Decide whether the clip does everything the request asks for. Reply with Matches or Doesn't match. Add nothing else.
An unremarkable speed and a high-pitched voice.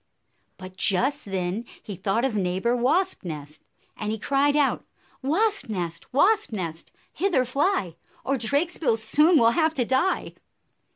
Matches